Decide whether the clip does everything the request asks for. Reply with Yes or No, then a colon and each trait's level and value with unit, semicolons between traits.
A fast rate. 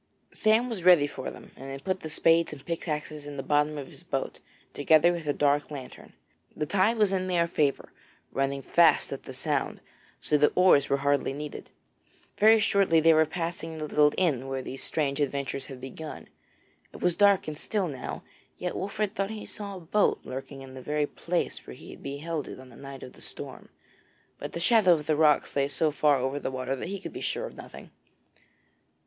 Yes: fast, 210 wpm